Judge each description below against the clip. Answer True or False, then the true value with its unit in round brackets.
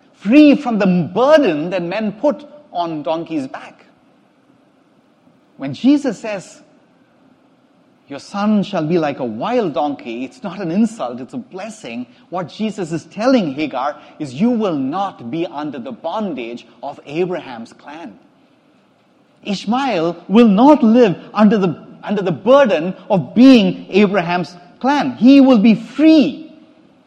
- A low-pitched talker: False (230 Hz)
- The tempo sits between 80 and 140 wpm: True (135 wpm)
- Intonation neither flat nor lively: False (6.6 semitones)